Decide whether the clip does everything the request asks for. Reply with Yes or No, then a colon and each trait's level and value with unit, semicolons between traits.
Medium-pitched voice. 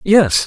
Yes: medium, 180 Hz